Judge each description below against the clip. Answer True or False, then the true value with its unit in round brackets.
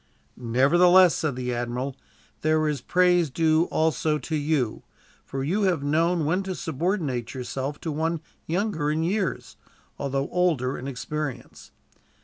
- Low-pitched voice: False (155 Hz)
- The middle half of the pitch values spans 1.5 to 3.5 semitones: False (4.1 semitones)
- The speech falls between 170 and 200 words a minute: False (135 wpm)